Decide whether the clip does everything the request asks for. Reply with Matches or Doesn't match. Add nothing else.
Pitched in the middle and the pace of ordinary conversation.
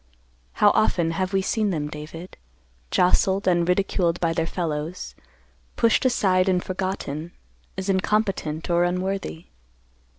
Doesn't match